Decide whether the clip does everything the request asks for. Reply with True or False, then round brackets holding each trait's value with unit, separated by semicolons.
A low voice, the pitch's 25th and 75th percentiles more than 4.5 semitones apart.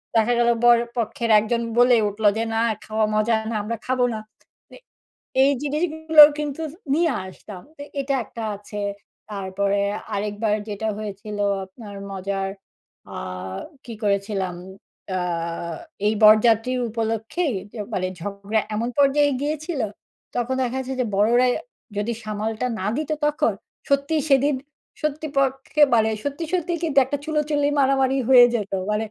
False (235 Hz; 4.9 semitones)